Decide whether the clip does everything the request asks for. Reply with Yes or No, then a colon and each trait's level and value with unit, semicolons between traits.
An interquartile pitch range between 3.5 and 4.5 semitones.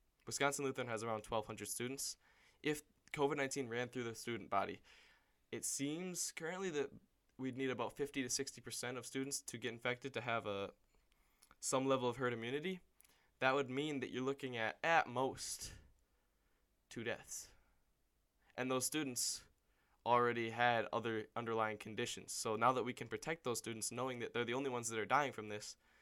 No: average, 3.0 semitones